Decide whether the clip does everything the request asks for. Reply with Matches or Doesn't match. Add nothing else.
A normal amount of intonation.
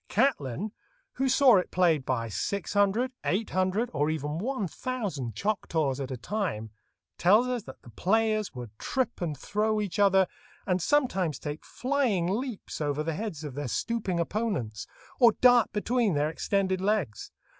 Doesn't match